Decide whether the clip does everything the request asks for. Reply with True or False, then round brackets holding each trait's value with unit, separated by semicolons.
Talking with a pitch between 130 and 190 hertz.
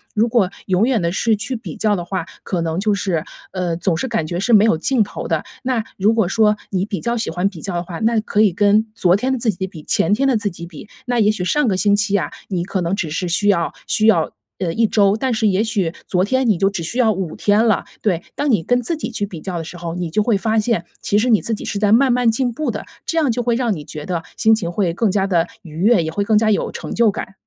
False (205 Hz)